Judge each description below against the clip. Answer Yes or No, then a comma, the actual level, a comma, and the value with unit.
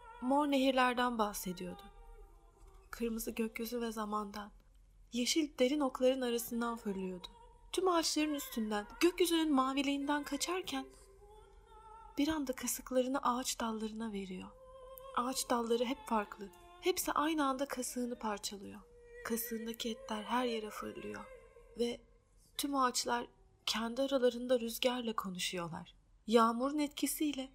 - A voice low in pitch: No, very high, 255 Hz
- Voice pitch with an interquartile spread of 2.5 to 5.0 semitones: Yes, average, 4.5 semitones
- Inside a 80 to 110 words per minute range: Yes, average, 100 wpm